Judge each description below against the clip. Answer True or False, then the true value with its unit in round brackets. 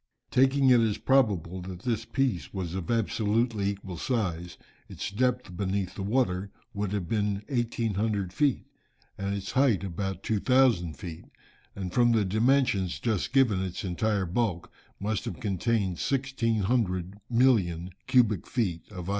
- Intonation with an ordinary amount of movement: True (4.3 semitones)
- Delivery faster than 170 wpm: False (145 wpm)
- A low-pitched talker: True (105 Hz)